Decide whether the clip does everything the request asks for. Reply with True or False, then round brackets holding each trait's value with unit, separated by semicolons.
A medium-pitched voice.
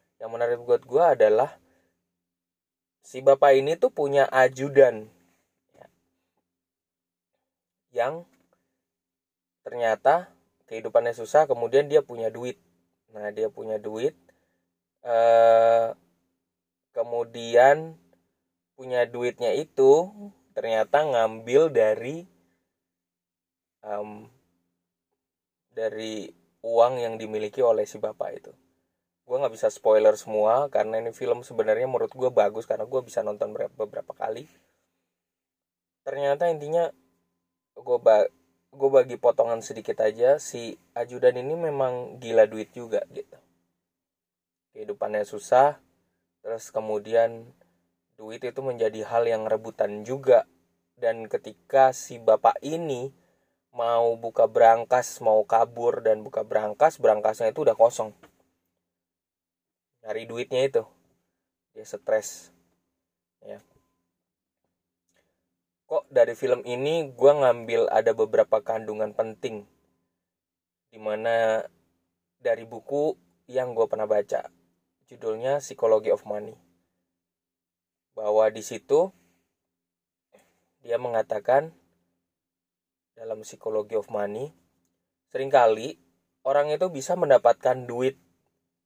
False (110 Hz)